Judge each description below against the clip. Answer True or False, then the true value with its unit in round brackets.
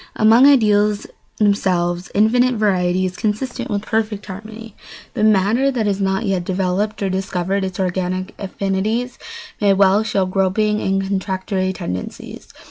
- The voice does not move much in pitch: True (2.3 semitones)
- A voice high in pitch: True (200 Hz)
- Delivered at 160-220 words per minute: False (135 wpm)